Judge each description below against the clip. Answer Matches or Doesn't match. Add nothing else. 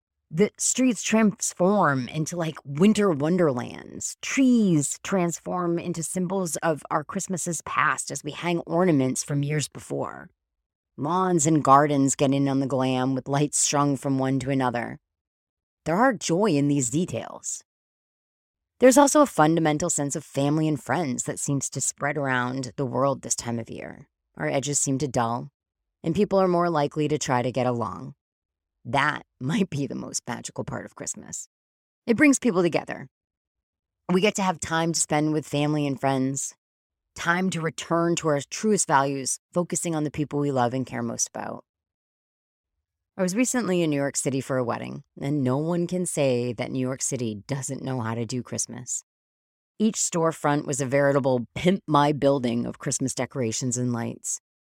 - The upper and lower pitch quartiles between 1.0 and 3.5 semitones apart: Doesn't match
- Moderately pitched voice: Matches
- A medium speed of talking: Matches